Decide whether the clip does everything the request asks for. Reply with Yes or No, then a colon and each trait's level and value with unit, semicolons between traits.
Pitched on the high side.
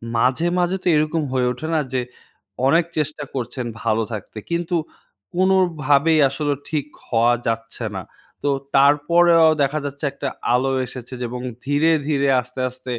No: medium, 140 Hz